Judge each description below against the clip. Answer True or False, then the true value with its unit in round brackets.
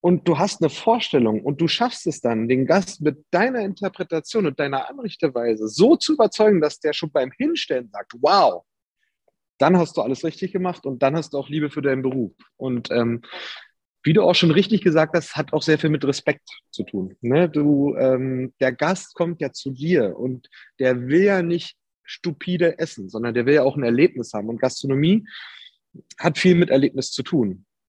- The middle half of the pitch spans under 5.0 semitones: False (5.3 semitones)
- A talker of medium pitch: True (155 Hz)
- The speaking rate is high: True (200 wpm)